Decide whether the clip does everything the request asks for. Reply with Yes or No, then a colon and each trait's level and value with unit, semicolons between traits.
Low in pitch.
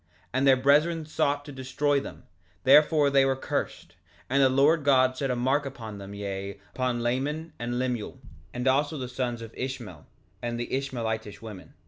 Yes: low, 130 Hz